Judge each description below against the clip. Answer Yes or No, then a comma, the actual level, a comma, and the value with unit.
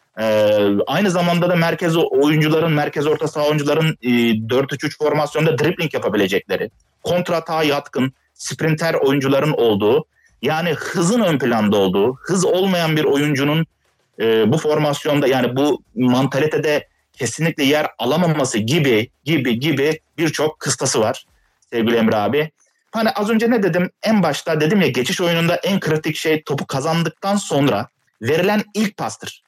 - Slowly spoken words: No, average, 135 wpm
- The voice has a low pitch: No, medium, 155 Hz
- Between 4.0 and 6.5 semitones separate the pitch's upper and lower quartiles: No, average, 3.2 semitones